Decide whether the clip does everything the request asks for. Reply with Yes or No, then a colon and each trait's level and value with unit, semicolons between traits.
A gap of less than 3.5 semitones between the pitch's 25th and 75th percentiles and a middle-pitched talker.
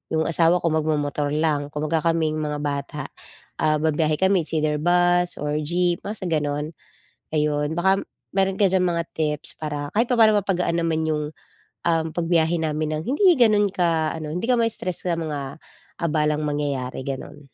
Yes: average, 2.9 semitones; medium, 160 Hz